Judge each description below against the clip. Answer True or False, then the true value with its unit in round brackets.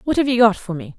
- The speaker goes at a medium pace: False (365 wpm)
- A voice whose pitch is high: True (215 Hz)